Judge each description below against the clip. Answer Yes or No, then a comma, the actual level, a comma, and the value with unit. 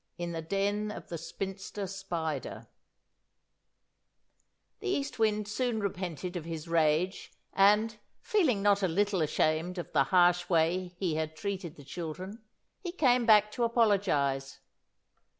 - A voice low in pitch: No, high, 190 Hz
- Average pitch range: Yes, average, 4.2 semitones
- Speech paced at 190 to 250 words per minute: No, slow, 135 wpm